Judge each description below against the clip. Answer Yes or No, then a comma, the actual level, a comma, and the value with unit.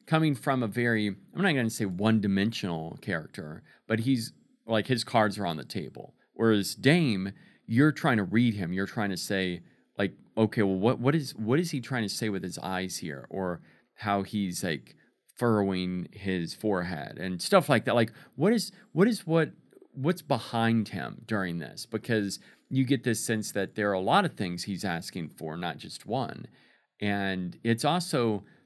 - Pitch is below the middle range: Yes, low, 110 Hz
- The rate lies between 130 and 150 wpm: No, average, 190 wpm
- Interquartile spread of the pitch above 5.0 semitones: Yes, wide, 5.6 semitones